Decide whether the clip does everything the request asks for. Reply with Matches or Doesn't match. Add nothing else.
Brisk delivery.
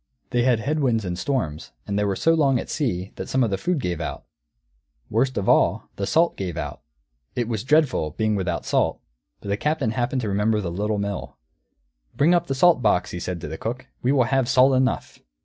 Matches